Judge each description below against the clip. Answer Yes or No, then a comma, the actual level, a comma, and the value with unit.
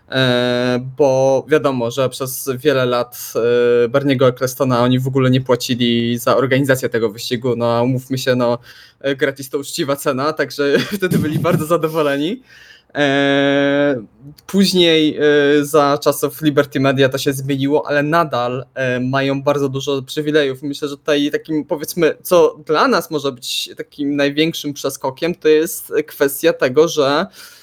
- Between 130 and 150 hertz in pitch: Yes, medium, 140 Hz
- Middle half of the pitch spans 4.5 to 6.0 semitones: No, average, 2.7 semitones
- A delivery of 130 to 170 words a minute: Yes, average, 135 wpm